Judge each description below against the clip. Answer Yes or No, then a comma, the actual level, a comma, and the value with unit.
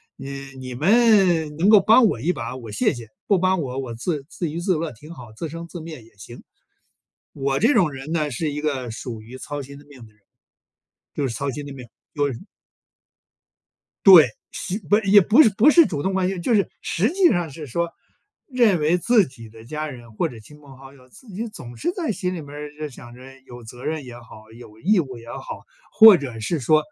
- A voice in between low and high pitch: Yes, medium, 150 Hz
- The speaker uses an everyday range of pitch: No, wide, 6.5 semitones